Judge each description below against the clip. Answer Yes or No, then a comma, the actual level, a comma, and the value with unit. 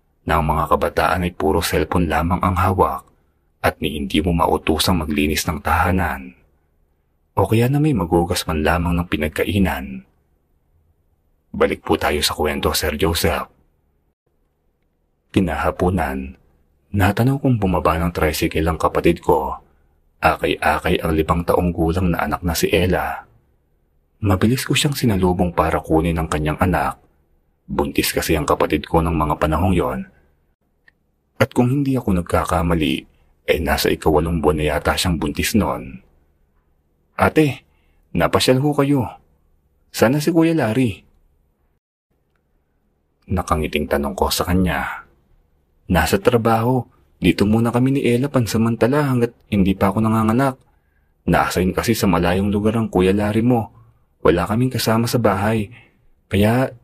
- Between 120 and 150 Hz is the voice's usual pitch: No, very low, 85 Hz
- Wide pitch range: Yes, wide, 6.4 semitones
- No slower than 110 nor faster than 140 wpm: Yes, average, 135 wpm